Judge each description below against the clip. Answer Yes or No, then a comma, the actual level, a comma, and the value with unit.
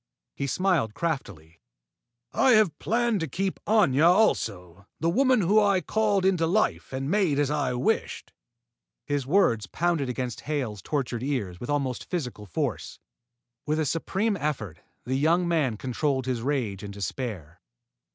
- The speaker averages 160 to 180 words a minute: No, average, 150 wpm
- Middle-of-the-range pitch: Yes, medium, 145 Hz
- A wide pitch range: Yes, wide, 6.8 semitones